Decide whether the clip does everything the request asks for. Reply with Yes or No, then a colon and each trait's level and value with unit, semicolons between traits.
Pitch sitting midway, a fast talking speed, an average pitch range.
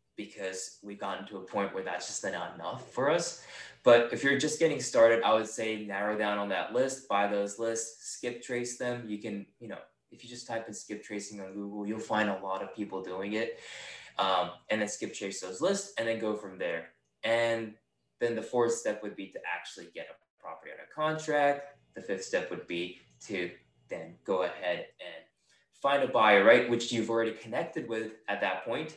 No: low, 110 Hz; fast, 215 wpm; average, 3.3 semitones